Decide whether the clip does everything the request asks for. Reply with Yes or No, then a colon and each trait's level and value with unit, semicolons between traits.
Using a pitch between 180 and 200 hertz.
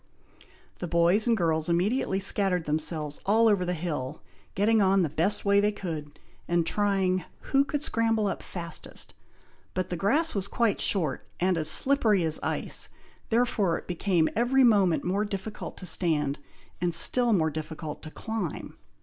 Yes: medium, 185 Hz